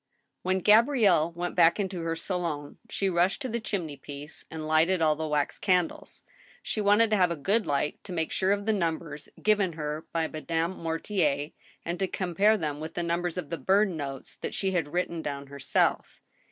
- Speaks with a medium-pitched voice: Yes, medium, 170 Hz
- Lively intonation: No, average, 3.8 semitones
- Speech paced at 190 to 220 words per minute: Yes, average, 200 wpm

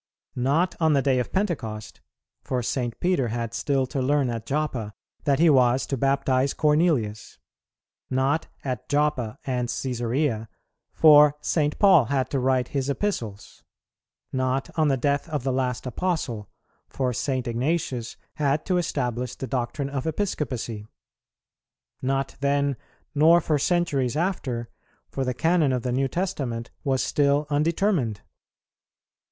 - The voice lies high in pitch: No, low, 135 Hz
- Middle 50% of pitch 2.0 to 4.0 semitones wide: Yes, average, 3.3 semitones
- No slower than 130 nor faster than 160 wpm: Yes, average, 140 wpm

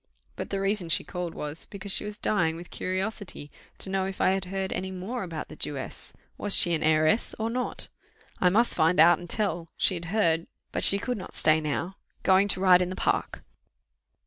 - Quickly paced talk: Yes, fast, 210 wpm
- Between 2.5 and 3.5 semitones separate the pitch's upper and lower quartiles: Yes, average, 3.1 semitones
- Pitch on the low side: No, medium, 185 Hz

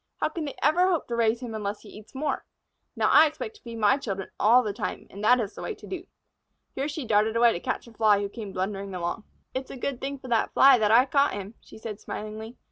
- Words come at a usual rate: No, fast, 260 wpm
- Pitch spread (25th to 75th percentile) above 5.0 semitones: No, average, 4.6 semitones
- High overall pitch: Yes, high, 230 Hz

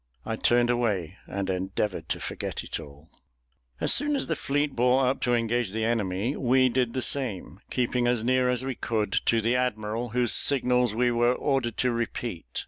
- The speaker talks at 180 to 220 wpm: Yes, average, 190 wpm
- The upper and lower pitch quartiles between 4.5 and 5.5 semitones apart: No, narrow, 2.5 semitones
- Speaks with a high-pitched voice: No, low, 120 Hz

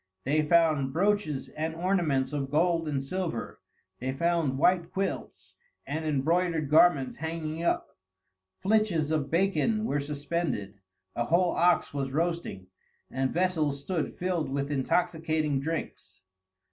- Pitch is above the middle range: No, medium, 160 Hz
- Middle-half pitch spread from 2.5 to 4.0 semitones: Yes, average, 3.7 semitones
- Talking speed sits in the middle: No, slow, 125 wpm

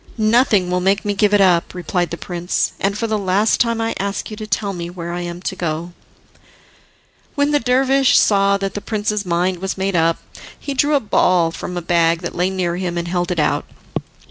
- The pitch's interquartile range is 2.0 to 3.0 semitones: No, average, 3.4 semitones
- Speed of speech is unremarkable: No, fast, 220 wpm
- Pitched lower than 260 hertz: Yes, high, 190 Hz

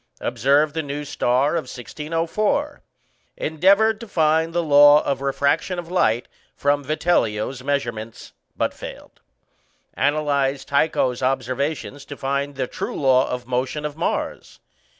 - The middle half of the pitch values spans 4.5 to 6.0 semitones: No, average, 3.2 semitones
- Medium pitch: Yes, medium, 145 Hz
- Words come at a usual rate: No, slow, 130 wpm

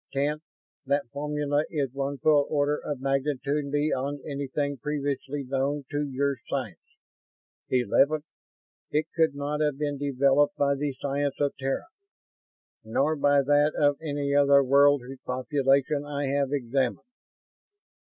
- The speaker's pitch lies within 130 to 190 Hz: Yes, medium, 140 Hz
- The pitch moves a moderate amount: No, narrow, 1.1 semitones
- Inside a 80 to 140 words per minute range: Yes, slow, 135 wpm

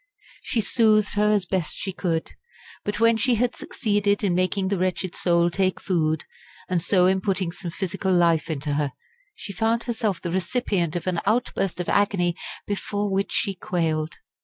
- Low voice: No, high, 190 Hz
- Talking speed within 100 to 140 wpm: No, average, 175 wpm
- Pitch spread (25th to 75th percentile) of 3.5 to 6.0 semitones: No, average, 3.1 semitones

